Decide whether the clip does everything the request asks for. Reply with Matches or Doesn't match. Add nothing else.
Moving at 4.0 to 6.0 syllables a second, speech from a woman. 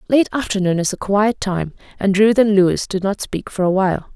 Matches